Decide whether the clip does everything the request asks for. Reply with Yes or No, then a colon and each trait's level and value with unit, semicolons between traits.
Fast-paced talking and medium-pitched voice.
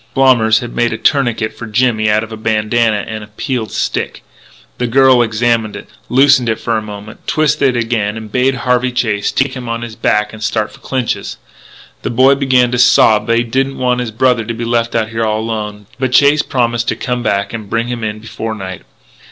No: fast, 215 wpm; low, 115 Hz